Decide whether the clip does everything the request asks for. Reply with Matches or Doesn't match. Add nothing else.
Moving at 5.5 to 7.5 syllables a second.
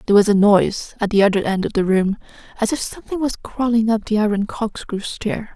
Matches